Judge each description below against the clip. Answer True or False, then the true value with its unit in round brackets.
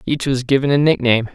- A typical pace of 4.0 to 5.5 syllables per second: False (6.7 syllables/s)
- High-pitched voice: False (130 Hz)